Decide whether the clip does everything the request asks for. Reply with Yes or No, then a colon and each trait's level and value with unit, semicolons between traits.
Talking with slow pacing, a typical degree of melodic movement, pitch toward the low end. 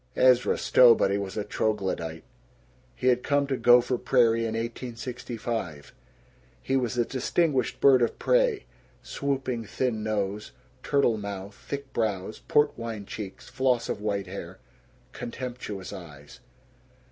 Yes: slow, 125 wpm; average, 4.1 semitones; low, 115 Hz